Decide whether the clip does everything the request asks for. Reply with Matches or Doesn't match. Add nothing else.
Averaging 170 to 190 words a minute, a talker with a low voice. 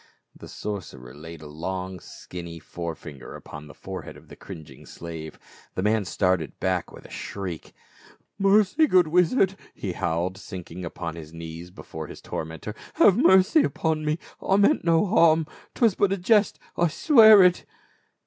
Matches